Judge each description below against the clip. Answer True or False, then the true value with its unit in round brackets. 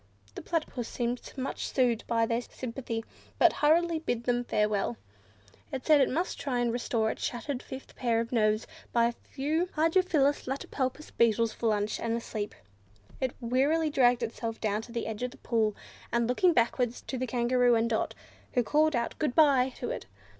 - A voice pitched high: True (245 Hz)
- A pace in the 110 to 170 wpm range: False (185 wpm)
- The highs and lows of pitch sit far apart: False (3.1 semitones)